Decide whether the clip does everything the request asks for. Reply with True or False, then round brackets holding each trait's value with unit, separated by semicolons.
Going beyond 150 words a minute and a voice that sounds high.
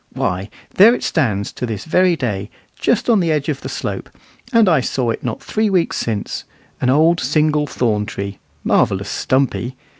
False (180 wpm; 140 Hz)